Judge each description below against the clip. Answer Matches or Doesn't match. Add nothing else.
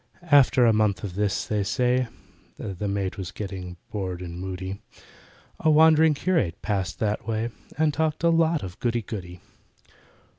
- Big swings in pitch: Matches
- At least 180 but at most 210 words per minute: Doesn't match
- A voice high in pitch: Doesn't match